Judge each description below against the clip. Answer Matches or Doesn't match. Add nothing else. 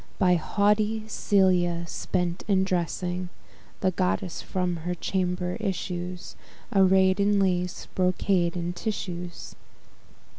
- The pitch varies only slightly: Matches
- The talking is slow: Matches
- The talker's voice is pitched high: Doesn't match